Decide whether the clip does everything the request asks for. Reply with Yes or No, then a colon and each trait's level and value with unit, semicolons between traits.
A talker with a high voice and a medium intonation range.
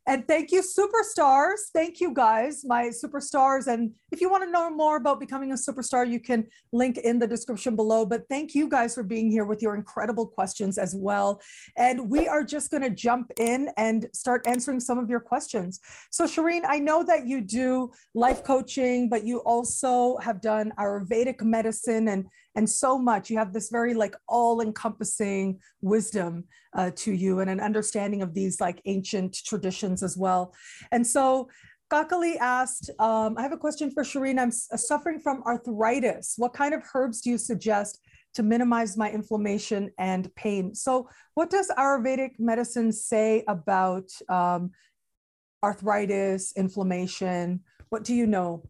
Yes: high, 235 Hz; average, 4.2 semitones